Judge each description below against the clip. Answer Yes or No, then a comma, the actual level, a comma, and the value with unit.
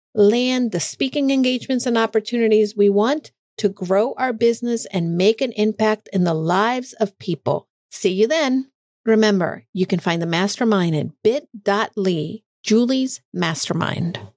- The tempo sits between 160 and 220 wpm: No, average, 140 wpm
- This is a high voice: Yes, high, 215 Hz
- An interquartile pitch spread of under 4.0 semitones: No, average, 4.6 semitones